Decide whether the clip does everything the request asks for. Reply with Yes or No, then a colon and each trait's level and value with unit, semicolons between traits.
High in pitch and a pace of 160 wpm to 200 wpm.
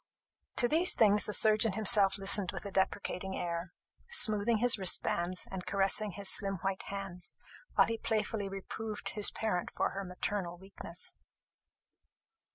No: high, 200 Hz; average, 145 wpm